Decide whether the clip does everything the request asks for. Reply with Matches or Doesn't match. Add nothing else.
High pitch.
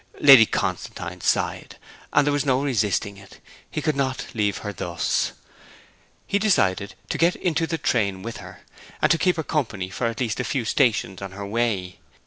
Doesn't match